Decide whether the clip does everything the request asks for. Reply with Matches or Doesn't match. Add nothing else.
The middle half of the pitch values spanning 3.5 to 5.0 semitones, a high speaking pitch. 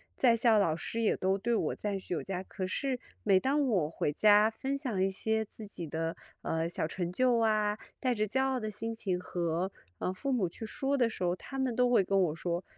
Matches